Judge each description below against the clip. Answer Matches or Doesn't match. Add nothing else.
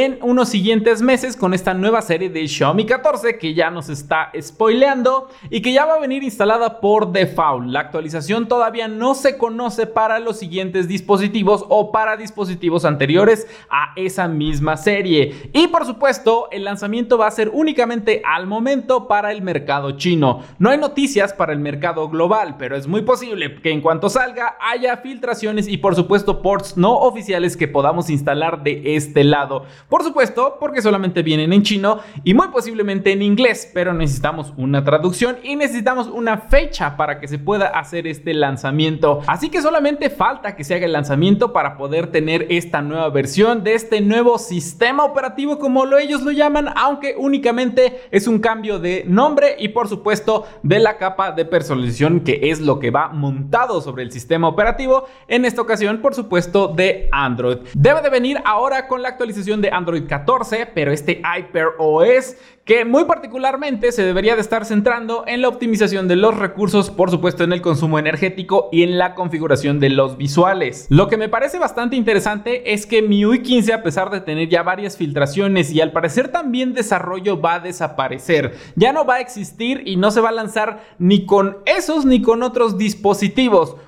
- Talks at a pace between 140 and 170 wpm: Doesn't match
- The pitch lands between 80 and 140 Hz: Doesn't match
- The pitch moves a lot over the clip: Matches